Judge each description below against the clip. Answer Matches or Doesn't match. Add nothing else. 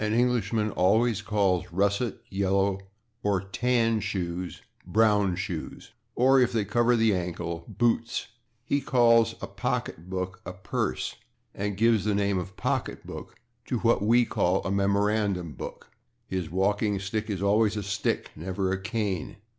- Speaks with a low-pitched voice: Matches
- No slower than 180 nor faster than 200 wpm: Doesn't match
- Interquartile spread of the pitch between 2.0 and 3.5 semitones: Matches